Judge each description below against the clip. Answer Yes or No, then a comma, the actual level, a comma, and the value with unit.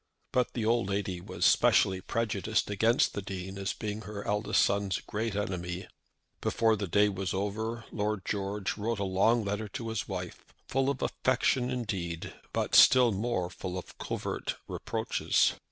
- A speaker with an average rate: Yes, average, 160 wpm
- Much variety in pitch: No, average, 2.8 semitones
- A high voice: No, low, 105 Hz